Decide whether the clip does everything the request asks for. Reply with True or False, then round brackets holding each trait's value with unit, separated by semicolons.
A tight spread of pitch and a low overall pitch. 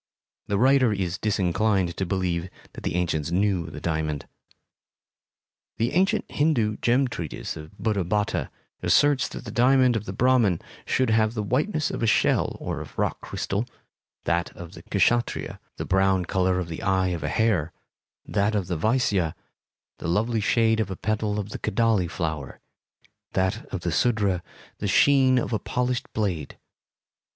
False (4.6 semitones; 105 Hz)